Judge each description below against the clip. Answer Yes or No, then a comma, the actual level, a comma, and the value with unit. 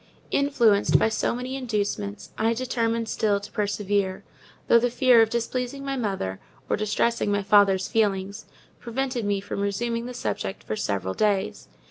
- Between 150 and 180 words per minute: Yes, average, 155 wpm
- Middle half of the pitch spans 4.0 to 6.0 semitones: No, average, 3.0 semitones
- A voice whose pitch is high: Yes, high, 215 Hz